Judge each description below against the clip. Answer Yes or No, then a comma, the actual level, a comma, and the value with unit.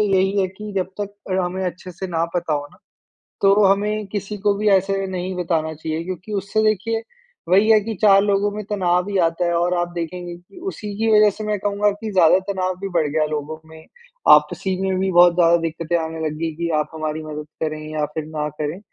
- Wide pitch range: No, average, 3.7 semitones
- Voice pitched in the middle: Yes, medium, 180 Hz